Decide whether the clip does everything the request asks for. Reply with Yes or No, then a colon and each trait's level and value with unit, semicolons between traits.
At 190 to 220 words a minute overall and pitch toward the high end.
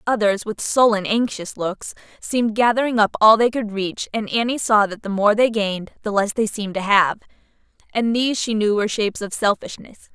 Yes: average, 200 wpm; high, 215 Hz